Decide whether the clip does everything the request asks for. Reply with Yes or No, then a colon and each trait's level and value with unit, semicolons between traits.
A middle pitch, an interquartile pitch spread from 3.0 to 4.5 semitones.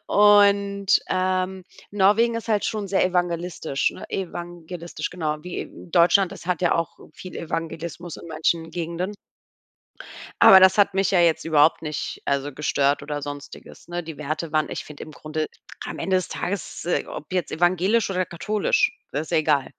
Yes: medium, 175 Hz; average, 3.3 semitones